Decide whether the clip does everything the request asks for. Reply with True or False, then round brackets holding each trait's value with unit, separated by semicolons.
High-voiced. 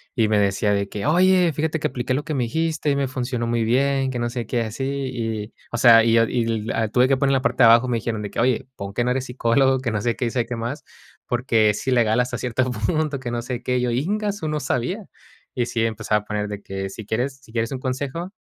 False (125 Hz)